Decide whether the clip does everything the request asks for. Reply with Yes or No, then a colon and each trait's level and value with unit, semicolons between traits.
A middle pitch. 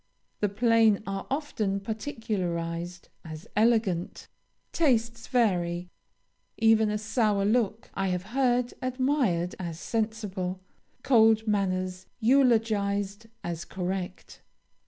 No: high, 210 Hz